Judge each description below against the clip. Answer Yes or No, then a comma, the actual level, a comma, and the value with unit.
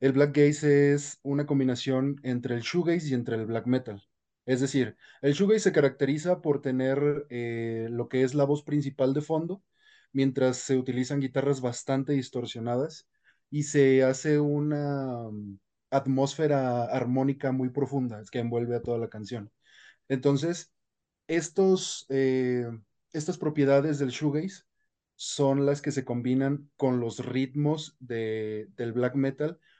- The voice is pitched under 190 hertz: Yes, low, 135 Hz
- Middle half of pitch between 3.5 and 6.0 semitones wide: No, average, 2.9 semitones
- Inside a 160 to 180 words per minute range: No, average, 145 wpm